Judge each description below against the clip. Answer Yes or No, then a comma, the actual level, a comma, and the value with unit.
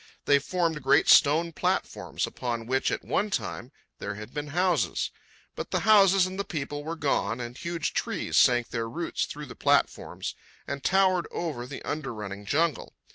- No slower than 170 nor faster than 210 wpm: Yes, average, 175 wpm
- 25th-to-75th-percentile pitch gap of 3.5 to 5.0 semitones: No, wide, 5.6 semitones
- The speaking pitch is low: No, medium, 145 Hz